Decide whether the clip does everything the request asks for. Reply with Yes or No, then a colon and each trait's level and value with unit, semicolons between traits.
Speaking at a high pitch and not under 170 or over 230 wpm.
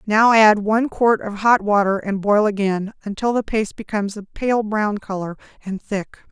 Yes: high, 210 Hz; average, 190 wpm